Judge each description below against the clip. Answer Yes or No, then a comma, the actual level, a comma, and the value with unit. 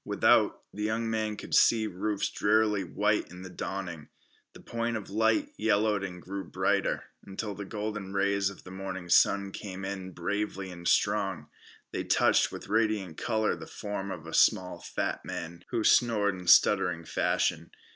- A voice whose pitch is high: No, low, 100 Hz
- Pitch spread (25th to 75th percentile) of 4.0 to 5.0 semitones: No, narrow, 2.4 semitones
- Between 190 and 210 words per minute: No, average, 165 wpm